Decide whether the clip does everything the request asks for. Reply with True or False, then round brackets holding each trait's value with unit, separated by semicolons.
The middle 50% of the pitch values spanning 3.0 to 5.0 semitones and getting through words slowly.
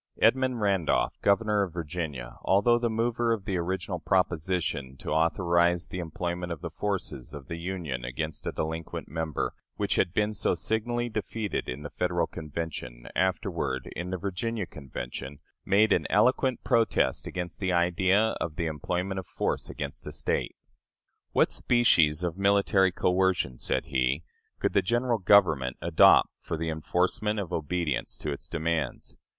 False (4.2 semitones; 155 wpm)